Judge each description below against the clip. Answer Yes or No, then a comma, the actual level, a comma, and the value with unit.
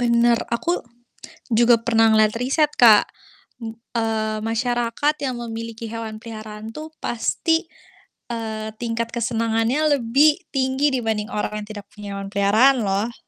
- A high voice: Yes, high, 230 Hz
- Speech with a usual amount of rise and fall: No, narrow, 2.1 semitones